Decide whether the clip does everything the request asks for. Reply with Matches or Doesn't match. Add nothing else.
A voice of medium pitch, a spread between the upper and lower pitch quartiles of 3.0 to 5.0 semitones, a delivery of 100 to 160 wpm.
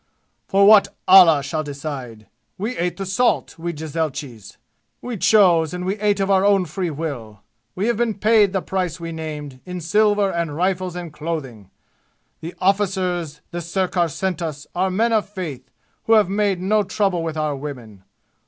Doesn't match